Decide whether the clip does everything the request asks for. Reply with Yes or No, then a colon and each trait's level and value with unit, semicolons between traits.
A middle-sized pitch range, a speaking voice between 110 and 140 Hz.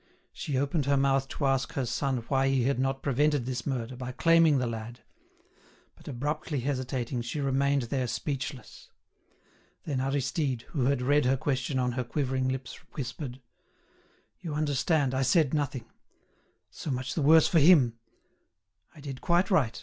No: narrow, 2.3 semitones; low, 135 Hz